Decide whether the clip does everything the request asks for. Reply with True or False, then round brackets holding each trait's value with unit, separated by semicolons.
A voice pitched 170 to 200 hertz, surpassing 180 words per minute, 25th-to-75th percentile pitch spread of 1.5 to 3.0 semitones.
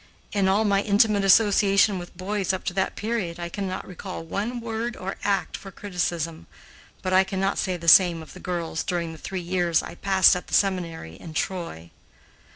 True (185 Hz; 190 wpm; 2.6 semitones)